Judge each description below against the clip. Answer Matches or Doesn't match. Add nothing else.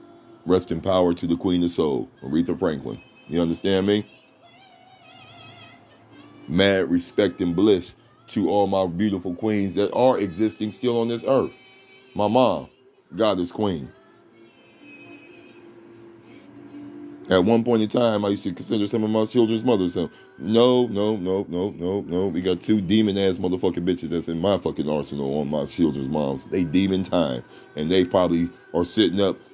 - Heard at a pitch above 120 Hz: Doesn't match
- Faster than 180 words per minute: Doesn't match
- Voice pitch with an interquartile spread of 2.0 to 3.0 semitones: Doesn't match